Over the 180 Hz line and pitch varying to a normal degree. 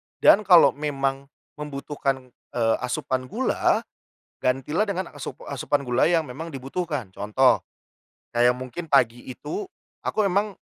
No: medium, 140 Hz; average, 4.5 semitones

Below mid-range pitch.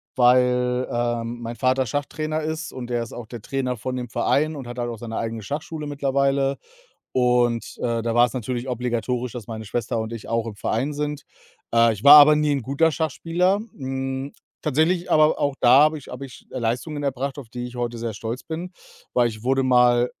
Yes: low, 125 Hz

